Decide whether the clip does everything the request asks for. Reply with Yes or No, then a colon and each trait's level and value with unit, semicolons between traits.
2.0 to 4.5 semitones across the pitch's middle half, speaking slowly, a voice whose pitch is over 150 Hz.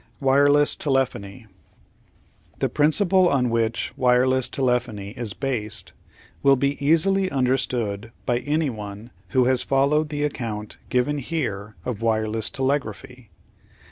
No: average, 4.0 semitones; slow, 110 wpm; low, 130 Hz